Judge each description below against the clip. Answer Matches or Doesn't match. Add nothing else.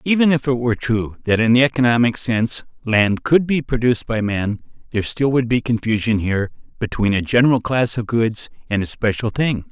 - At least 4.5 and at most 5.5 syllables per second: Doesn't match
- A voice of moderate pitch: Doesn't match